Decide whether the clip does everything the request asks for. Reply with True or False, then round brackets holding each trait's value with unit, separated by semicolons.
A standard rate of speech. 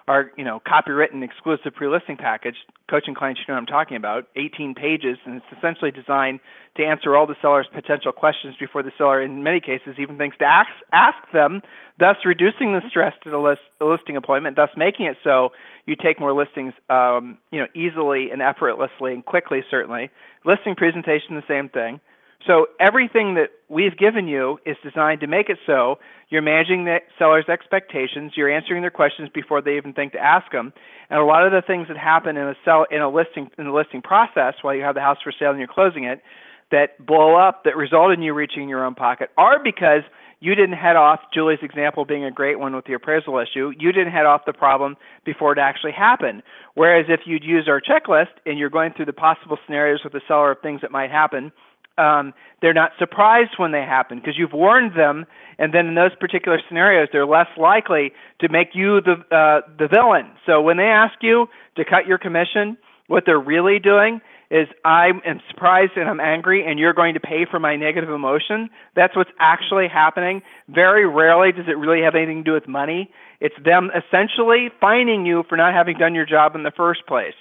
False (210 wpm)